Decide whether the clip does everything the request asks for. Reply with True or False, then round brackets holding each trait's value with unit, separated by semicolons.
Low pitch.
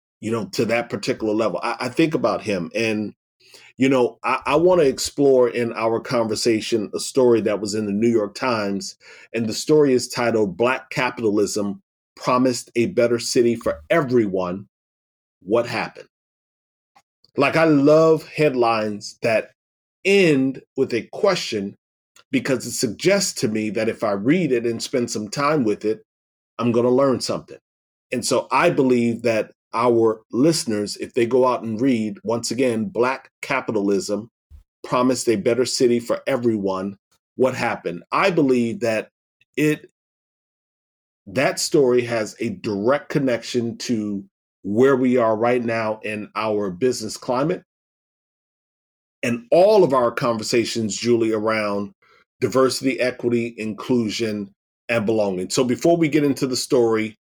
True (115 Hz)